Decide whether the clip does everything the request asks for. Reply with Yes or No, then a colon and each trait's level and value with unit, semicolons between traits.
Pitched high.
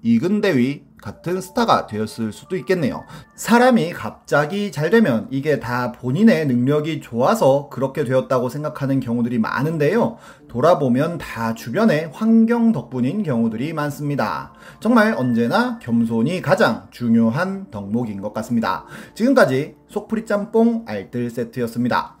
No: medium, 145 Hz